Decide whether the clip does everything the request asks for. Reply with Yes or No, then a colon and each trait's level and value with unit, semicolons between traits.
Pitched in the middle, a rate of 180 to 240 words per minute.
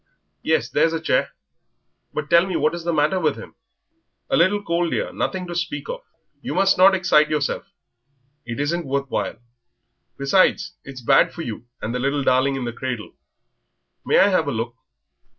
Yes: medium, 155 Hz; average, 185 wpm